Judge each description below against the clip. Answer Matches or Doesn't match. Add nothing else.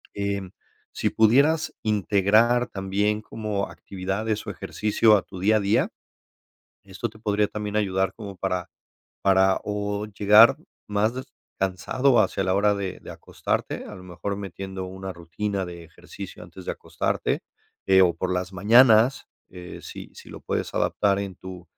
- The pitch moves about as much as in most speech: Doesn't match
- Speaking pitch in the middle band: Doesn't match